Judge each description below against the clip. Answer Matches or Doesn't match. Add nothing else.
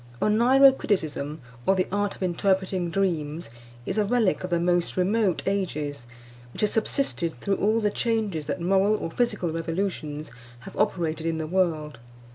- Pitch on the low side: Doesn't match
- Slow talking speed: Doesn't match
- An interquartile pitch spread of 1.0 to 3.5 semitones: Doesn't match